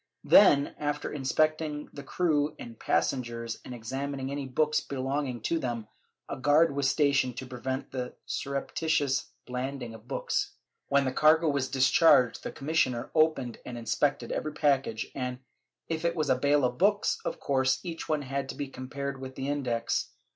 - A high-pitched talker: No, medium, 140 Hz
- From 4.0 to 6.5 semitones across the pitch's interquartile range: No, narrow, 2.5 semitones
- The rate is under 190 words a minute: Yes, average, 165 wpm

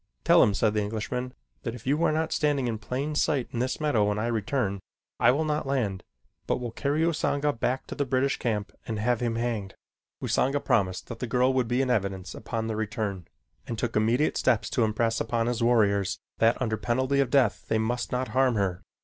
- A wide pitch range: No, average, 3.3 semitones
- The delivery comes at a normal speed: No, fast, 215 wpm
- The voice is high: No, low, 120 Hz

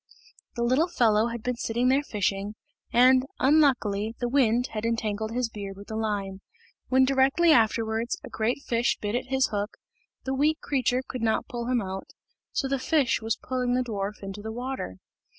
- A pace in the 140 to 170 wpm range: No, average, 185 wpm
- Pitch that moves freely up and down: No, average, 3.3 semitones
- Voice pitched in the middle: No, high, 235 Hz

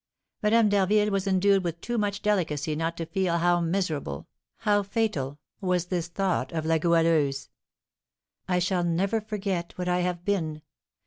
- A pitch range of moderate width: Yes, average, 3.4 semitones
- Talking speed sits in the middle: Yes, average, 155 wpm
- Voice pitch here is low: No, medium, 180 Hz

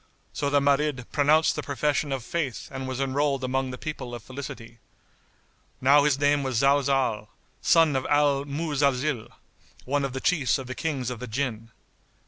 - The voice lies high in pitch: No, medium, 140 Hz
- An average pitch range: No, narrow, 2.1 semitones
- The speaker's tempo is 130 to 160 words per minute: No, average, 170 wpm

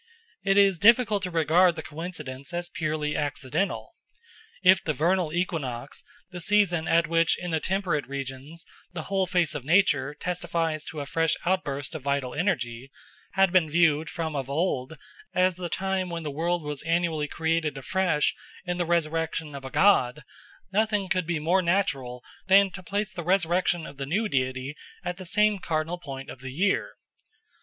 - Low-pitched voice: No, medium, 165 Hz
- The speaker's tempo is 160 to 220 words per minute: Yes, average, 170 wpm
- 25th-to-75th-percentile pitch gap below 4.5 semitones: Yes, average, 3.8 semitones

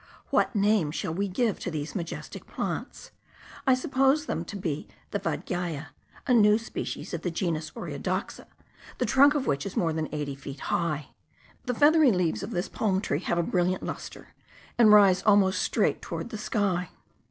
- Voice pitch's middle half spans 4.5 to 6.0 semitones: Yes, average, 5.0 semitones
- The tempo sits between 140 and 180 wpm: Yes, average, 175 wpm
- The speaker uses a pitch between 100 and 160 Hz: No, medium, 185 Hz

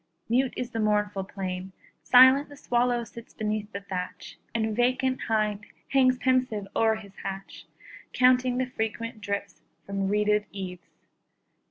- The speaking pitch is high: Yes, high, 220 Hz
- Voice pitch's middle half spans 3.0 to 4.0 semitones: Yes, average, 3.7 semitones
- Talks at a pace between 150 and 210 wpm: No, average, 140 wpm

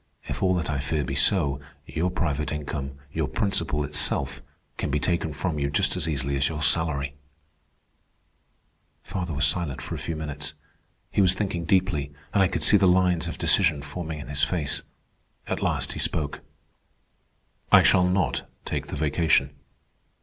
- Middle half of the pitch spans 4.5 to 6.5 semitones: No, average, 3.9 semitones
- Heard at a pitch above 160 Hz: No, very low, 80 Hz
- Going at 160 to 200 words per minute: Yes, average, 170 wpm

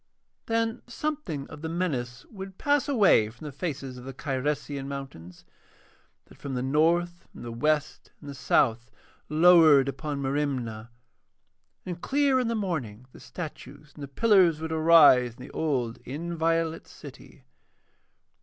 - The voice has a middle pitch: Yes, medium, 150 Hz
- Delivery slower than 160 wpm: Yes, average, 145 wpm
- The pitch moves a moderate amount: Yes, average, 4.7 semitones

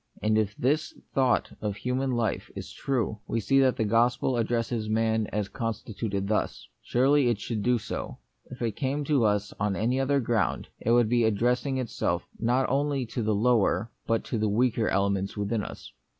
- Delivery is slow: No, average, 180 wpm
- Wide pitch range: No, average, 2.9 semitones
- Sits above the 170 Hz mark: No, low, 115 Hz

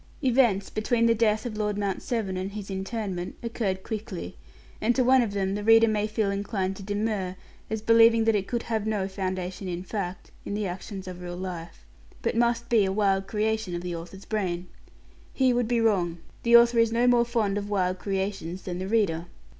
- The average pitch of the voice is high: Yes, high, 205 Hz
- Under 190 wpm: No, fast, 205 wpm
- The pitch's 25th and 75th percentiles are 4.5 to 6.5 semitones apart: No, average, 3.2 semitones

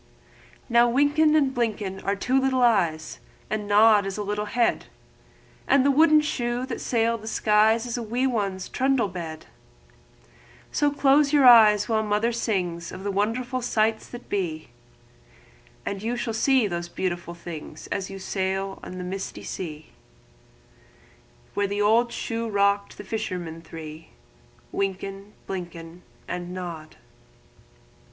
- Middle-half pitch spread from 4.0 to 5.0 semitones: Yes, average, 4.5 semitones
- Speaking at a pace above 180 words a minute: No, average, 140 wpm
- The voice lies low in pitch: No, high, 210 Hz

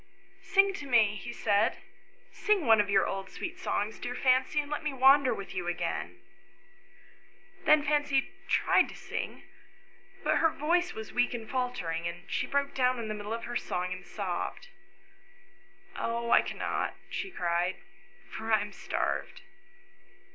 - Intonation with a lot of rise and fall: Yes, wide, 6.7 semitones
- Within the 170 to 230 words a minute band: Yes, average, 175 wpm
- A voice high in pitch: Yes, high, 245 Hz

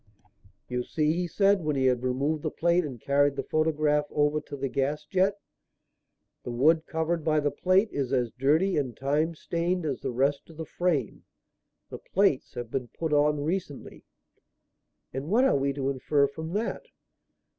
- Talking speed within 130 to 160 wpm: No, average, 175 wpm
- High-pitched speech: No, medium, 150 Hz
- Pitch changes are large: No, average, 3.3 semitones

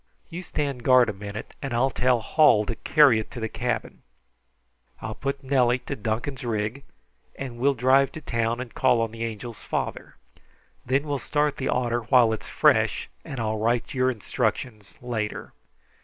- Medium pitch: No, low, 120 Hz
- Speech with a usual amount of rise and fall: Yes, average, 3.2 semitones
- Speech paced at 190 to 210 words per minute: No, average, 175 wpm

